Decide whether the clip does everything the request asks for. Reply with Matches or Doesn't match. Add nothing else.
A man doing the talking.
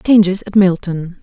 Doesn't match